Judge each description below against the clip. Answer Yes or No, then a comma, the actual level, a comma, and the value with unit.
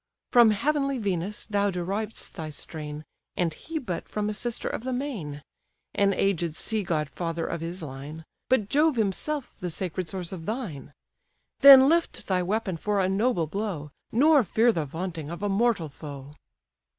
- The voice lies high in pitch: Yes, high, 195 Hz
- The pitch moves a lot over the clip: Yes, wide, 5.7 semitones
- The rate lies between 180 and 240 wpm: No, average, 170 wpm